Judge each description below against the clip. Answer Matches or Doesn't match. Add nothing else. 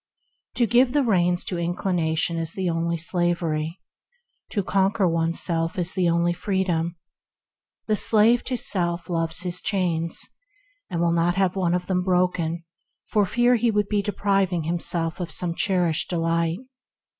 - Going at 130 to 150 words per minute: Matches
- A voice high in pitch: Doesn't match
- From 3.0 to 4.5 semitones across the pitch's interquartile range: Doesn't match